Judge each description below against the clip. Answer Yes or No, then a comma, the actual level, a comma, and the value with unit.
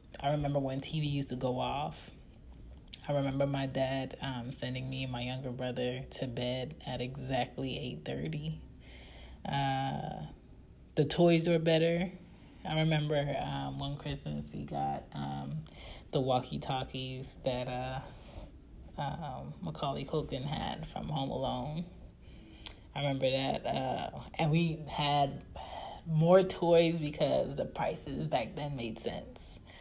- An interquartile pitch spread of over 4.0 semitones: No, average, 3.1 semitones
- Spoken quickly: No, slow, 135 wpm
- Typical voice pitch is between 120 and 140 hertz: Yes, low, 135 Hz